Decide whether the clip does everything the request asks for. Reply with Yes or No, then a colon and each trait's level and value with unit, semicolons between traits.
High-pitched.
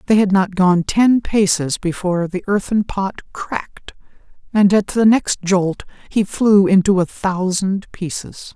Yes: high, 195 Hz